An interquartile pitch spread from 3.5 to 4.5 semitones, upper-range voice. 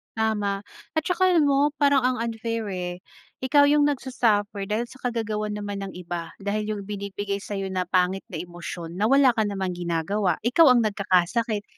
Yes: average, 3.9 semitones; high, 210 Hz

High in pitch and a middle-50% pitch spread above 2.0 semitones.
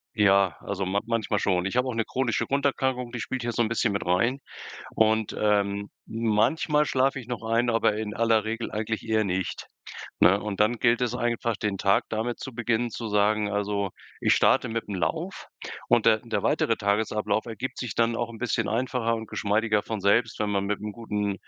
No: low, 110 Hz; narrow, 2.5 semitones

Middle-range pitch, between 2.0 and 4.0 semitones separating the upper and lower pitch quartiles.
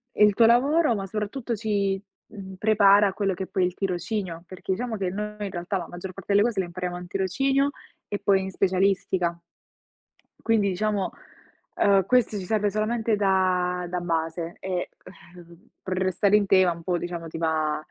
No: high, 195 Hz; average, 2.8 semitones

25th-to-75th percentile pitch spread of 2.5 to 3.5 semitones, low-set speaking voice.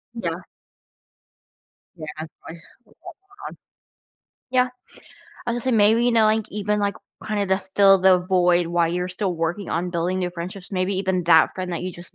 No: average, 2.8 semitones; medium, 185 Hz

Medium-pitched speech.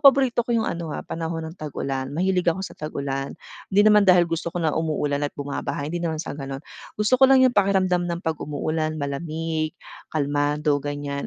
Yes: medium, 160 Hz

